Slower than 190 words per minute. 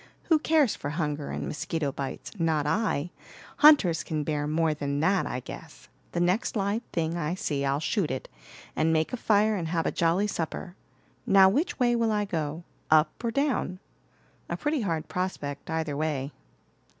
Yes: average, 175 wpm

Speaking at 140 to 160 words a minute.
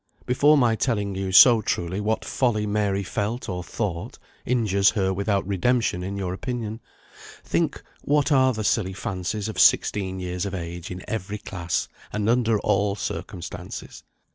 Yes: average, 155 wpm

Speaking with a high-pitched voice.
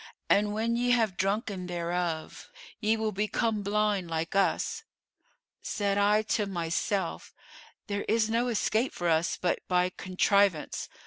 Yes: high, 200 Hz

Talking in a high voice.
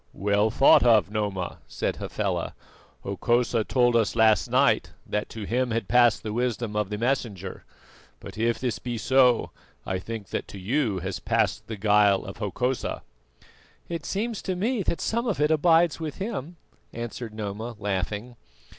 No: low, 115 Hz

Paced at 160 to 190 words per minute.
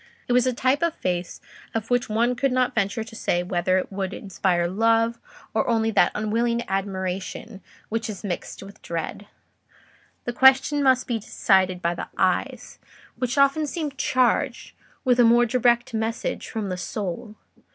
Yes: average, 165 wpm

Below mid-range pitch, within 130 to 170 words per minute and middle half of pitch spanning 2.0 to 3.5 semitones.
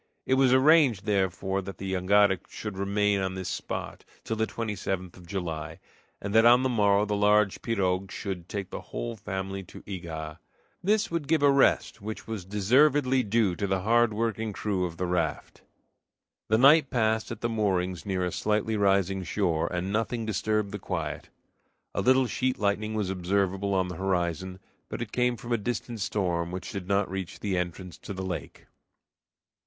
No: low, 100 Hz; average, 180 wpm; average, 3.2 semitones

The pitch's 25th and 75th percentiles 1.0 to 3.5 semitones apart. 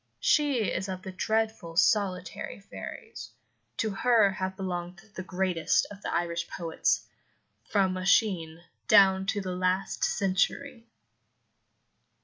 Yes: narrow, 2.6 semitones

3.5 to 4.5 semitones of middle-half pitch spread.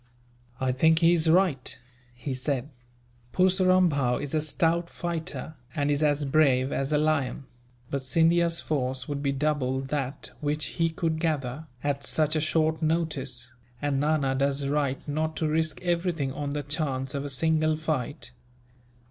No: average, 2.7 semitones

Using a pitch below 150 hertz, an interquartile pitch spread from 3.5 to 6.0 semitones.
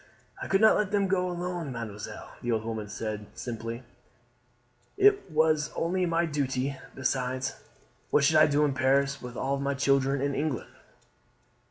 Yes: medium, 140 Hz; average, 4.6 semitones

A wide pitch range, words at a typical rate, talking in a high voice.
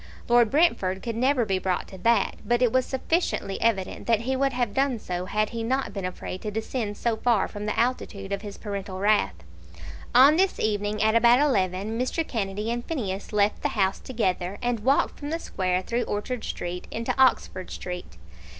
No: average, 4.1 semitones; average, 195 wpm; high, 220 Hz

